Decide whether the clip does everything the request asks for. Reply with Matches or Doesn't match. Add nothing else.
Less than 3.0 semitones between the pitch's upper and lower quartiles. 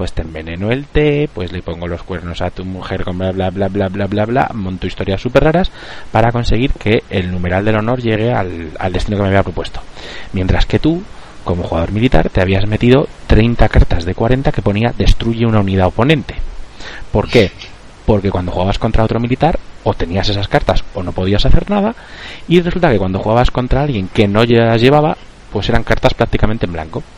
Doesn't match